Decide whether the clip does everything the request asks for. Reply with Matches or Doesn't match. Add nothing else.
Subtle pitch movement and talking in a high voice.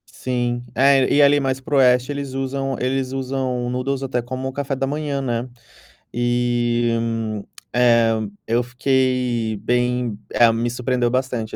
Doesn't match